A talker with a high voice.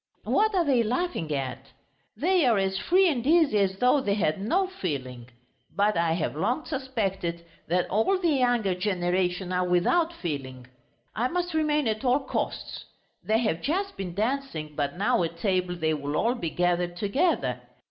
Yes: high, 200 Hz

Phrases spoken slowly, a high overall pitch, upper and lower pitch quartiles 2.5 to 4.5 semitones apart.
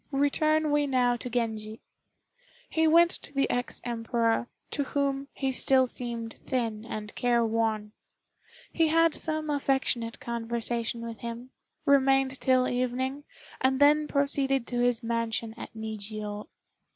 Yes: slow, 130 wpm; high, 245 Hz; average, 3.4 semitones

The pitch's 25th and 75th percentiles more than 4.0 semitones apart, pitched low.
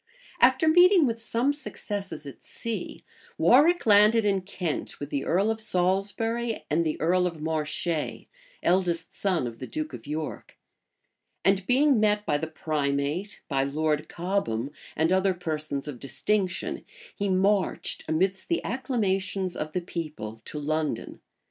No: wide, 5.4 semitones; medium, 185 Hz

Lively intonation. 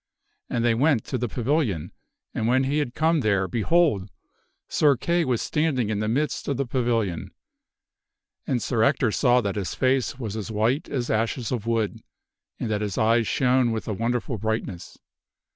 No: average, 3.5 semitones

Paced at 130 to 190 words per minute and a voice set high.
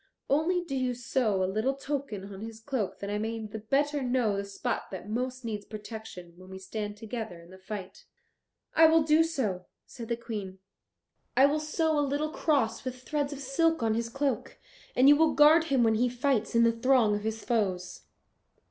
No: average, 200 wpm; high, 235 Hz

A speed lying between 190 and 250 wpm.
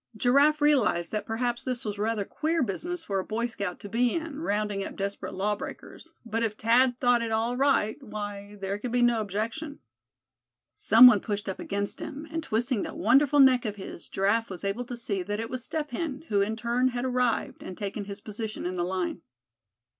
Yes: fast, 205 wpm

